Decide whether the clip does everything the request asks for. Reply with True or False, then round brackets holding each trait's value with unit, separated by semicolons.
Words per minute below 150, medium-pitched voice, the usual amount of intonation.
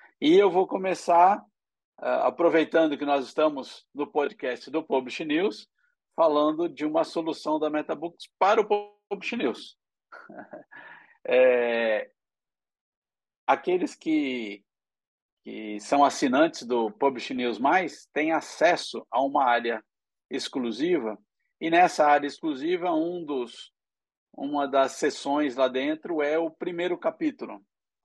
False (120 wpm; 160 Hz; 7.6 semitones)